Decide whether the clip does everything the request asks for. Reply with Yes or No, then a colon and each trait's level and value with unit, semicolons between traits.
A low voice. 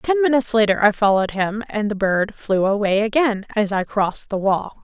No: high, 210 Hz